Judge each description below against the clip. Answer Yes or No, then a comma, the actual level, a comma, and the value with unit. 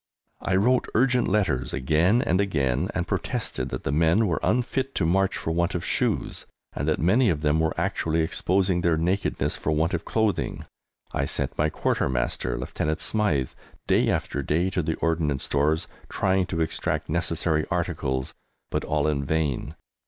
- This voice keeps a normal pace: Yes, average, 165 wpm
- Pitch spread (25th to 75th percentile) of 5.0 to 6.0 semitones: No, average, 4.0 semitones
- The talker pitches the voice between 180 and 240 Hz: No, very low, 80 Hz